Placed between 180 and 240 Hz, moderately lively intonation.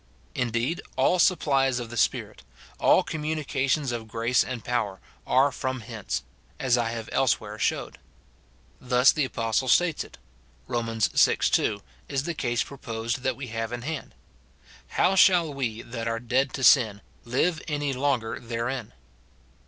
No: low, 125 Hz; average, 3.2 semitones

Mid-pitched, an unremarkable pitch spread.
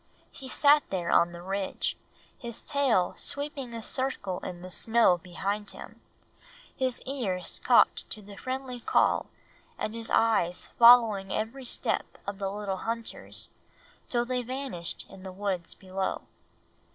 No: high, 215 Hz; average, 4.9 semitones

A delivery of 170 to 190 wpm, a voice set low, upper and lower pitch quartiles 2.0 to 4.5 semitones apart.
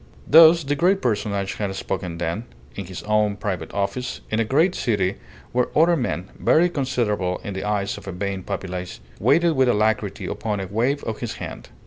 No: average, 185 wpm; low, 105 Hz; average, 5.2 semitones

